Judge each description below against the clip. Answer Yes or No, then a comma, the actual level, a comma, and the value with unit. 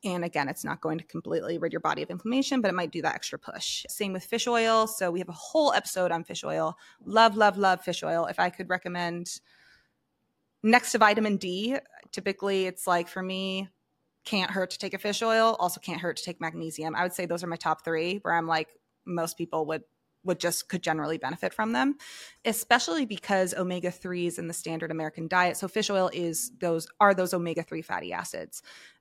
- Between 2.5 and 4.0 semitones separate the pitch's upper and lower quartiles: Yes, average, 3.6 semitones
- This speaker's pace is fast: Yes, fast, 210 wpm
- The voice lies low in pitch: No, medium, 180 Hz